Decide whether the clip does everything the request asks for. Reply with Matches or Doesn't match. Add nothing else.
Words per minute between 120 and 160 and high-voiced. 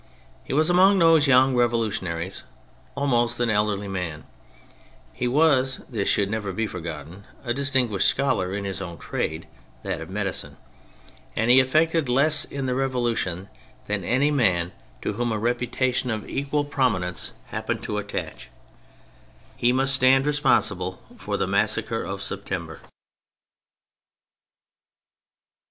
Doesn't match